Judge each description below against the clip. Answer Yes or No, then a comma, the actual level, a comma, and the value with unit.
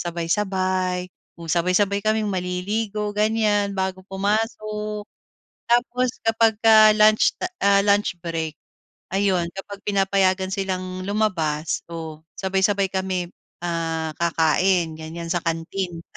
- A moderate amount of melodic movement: Yes, average, 3.2 semitones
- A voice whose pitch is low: No, high, 190 Hz